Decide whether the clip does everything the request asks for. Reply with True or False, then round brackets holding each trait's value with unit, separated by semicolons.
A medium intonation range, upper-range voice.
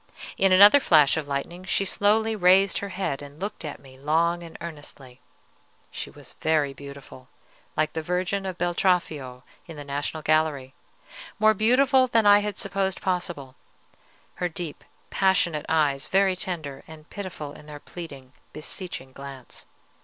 False (4.9 semitones; 165 Hz)